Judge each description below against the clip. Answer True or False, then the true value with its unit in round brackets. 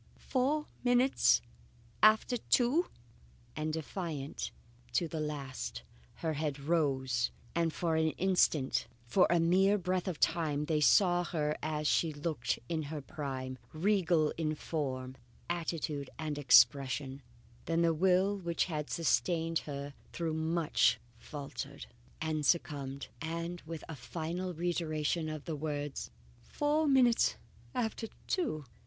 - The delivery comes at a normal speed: False (130 wpm)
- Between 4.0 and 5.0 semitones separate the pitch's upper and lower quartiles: False (3.3 semitones)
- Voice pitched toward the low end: False (160 Hz)